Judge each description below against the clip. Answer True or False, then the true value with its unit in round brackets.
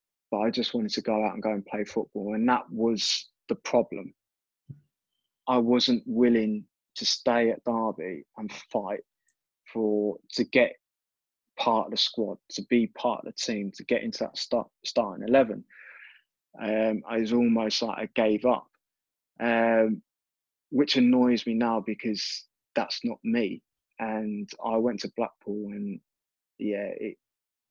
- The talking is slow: False (155 wpm)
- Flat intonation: True (2.3 semitones)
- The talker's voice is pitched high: False (115 Hz)